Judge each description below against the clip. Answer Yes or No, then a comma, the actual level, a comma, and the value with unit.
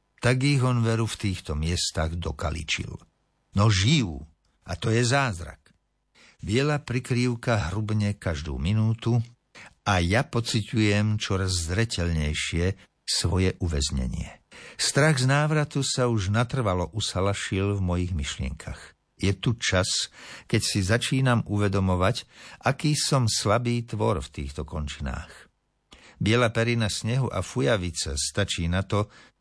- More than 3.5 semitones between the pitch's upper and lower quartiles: Yes, average, 5.1 semitones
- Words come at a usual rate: Yes, average, 120 wpm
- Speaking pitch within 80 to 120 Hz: Yes, low, 105 Hz